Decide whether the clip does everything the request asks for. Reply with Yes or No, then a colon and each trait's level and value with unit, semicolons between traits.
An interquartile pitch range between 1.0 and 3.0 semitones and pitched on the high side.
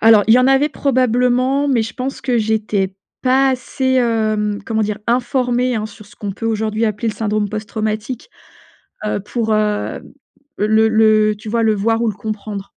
Yes: narrow, 2.6 semitones; high, 220 Hz